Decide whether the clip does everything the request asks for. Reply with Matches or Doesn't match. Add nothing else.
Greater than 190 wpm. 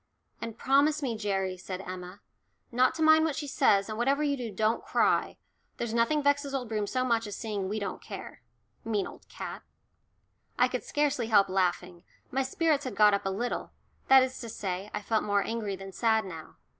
Matches